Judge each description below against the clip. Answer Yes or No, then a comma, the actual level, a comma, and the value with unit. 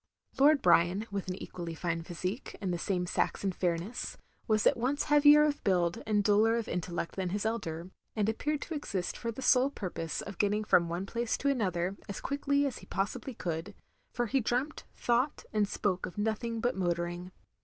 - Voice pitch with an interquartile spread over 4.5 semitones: Yes, average, 5.3 semitones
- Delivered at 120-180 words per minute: No, average, 190 wpm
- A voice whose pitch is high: Yes, high, 205 Hz